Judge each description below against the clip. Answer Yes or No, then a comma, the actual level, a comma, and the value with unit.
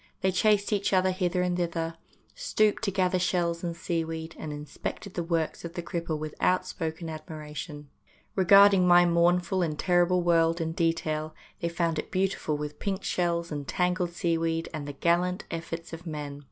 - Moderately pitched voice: Yes, medium, 170 Hz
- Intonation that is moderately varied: No, narrow, 2.0 semitones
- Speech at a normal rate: Yes, average, 175 wpm